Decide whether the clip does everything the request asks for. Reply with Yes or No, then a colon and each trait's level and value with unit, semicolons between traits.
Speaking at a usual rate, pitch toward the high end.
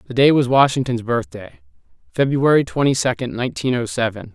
No: average, 150 wpm; low, 125 Hz